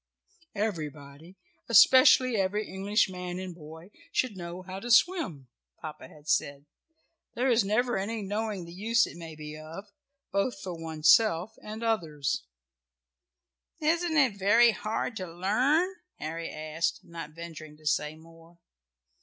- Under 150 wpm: Yes, average, 140 wpm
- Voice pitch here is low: No, medium, 185 Hz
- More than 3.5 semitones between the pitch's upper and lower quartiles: Yes, wide, 5.5 semitones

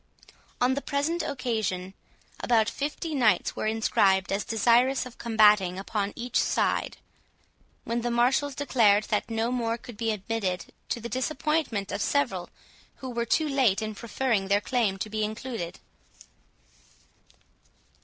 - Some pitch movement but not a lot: Yes, average, 3.6 semitones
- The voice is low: No, high, 230 Hz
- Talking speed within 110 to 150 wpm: Yes, average, 140 wpm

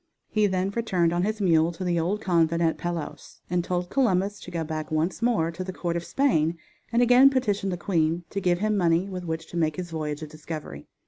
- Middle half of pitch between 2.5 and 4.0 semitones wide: Yes, average, 3.3 semitones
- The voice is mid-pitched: Yes, medium, 175 Hz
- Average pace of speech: No, fast, 230 wpm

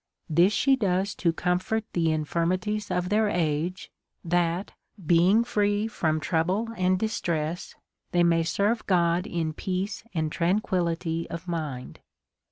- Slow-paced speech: Yes, slow, 130 wpm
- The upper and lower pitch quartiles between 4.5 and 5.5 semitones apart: No, average, 3.3 semitones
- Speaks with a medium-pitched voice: Yes, medium, 175 Hz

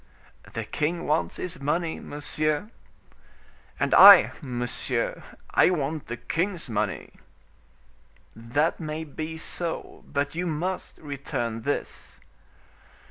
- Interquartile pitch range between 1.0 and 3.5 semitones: Yes, average, 3.2 semitones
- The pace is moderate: No, slow, 105 wpm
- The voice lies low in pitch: No, medium, 150 Hz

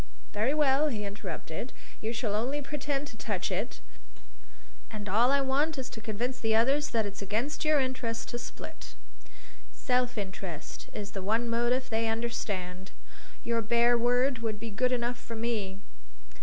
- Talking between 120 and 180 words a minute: Yes, average, 155 wpm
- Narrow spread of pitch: No, average, 3.4 semitones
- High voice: Yes, high, 235 Hz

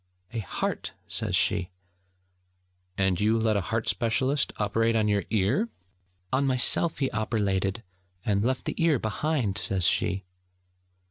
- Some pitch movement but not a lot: Yes, average, 4.4 semitones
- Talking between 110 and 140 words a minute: Yes, slow, 135 wpm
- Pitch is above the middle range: No, low, 110 Hz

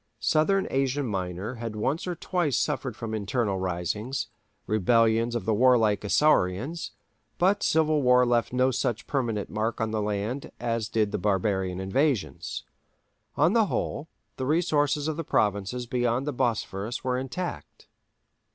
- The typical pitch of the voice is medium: No, low, 120 Hz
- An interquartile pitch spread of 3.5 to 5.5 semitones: Yes, average, 5.0 semitones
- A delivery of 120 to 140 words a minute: Yes, slow, 135 wpm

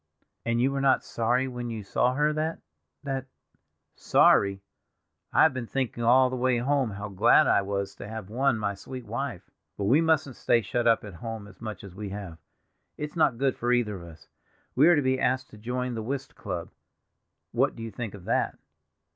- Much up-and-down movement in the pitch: No, average, 4.2 semitones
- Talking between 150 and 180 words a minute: No, average, 200 wpm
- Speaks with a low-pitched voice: Yes, low, 120 Hz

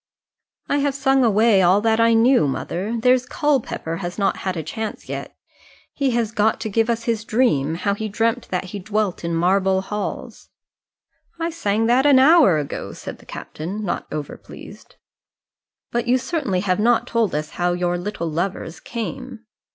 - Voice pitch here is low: No, high, 215 Hz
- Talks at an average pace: Yes, average, 175 wpm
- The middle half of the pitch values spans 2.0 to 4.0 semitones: No, average, 4.8 semitones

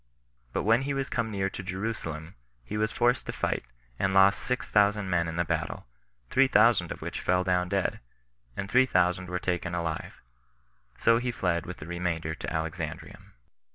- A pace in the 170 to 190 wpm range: Yes, average, 185 wpm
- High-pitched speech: No, very low, 95 Hz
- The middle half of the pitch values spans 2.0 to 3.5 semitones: No, average, 4.0 semitones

